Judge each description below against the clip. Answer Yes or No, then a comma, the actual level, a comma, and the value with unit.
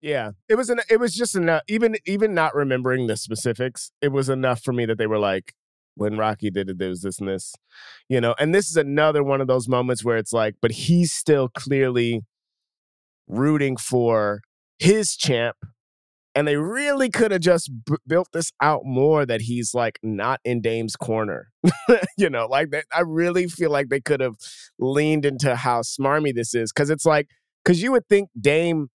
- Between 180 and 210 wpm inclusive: Yes, average, 200 wpm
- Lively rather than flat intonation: Yes, wide, 5.8 semitones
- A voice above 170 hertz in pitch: No, low, 135 Hz